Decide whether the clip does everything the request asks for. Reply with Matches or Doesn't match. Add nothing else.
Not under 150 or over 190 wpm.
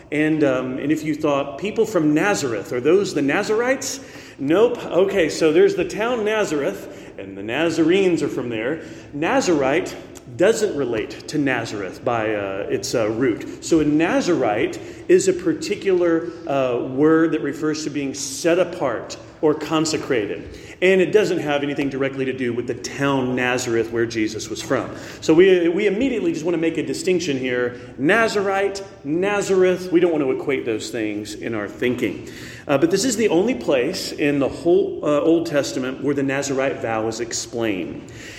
Matches